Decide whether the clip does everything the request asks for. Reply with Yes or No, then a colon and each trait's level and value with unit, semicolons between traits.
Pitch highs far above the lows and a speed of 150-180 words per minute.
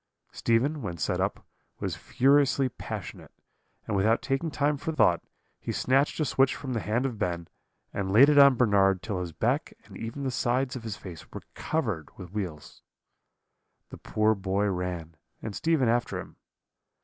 Yes: wide, 6.0 semitones; average, 175 wpm